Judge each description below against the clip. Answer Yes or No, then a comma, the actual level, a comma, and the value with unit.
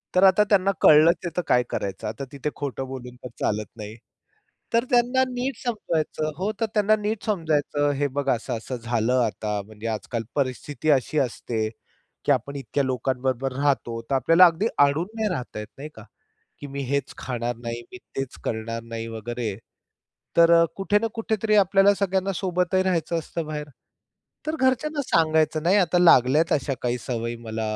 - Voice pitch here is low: No, medium, 145 Hz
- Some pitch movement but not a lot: No, wide, 7.5 semitones